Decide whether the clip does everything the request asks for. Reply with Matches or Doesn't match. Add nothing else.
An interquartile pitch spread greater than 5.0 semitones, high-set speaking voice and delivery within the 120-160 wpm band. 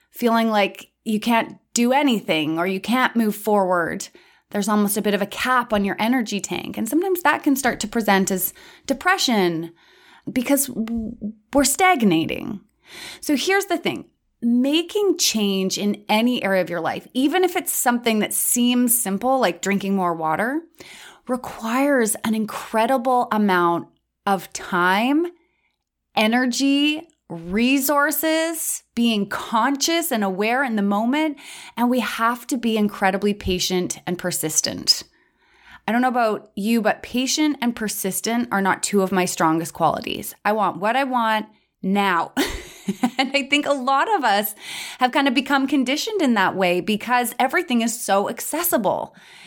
Matches